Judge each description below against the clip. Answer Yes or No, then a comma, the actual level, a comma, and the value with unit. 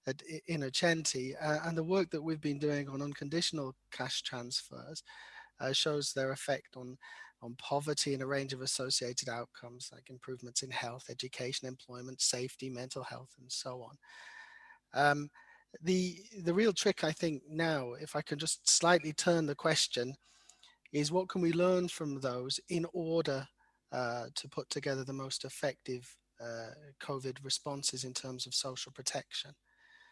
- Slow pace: No, average, 155 wpm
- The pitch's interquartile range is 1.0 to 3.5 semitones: No, average, 4.2 semitones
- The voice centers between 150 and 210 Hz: No, medium, 140 Hz